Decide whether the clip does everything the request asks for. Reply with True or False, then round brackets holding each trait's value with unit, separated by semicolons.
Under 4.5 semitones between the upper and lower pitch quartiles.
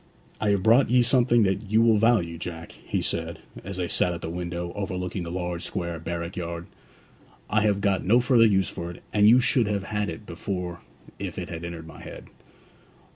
True (3.8 semitones)